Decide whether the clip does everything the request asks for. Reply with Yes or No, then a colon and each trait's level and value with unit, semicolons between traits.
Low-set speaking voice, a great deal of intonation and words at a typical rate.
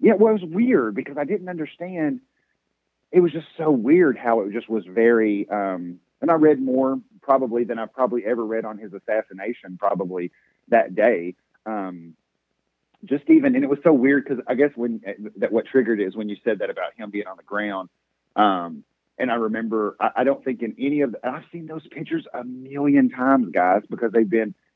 No: low, 125 Hz; wide, 5.7 semitones; fast, 210 wpm